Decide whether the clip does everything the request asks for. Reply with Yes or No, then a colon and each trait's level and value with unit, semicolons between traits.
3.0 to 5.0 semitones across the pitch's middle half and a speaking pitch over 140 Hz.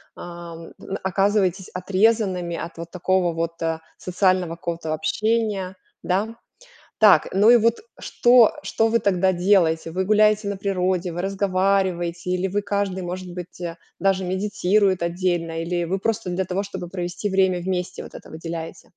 No: narrow, 2.4 semitones; medium, 185 Hz